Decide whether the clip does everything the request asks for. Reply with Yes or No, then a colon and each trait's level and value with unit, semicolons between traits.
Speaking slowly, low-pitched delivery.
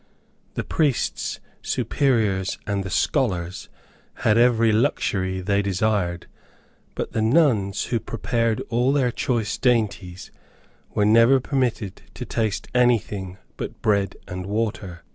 Yes: slow, 120 wpm; low, 110 Hz